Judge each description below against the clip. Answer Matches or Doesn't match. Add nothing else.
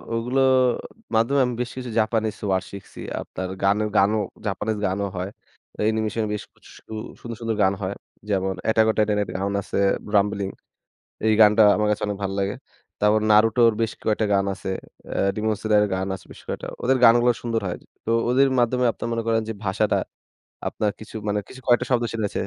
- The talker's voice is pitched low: Matches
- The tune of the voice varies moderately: Doesn't match